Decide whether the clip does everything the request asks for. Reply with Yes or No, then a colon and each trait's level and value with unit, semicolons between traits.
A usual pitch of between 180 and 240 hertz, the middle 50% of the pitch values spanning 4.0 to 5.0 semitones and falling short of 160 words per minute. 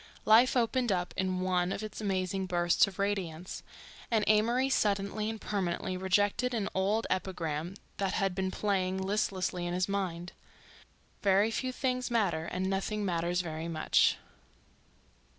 No: high, 190 Hz; average, 2.8 semitones; average, 145 wpm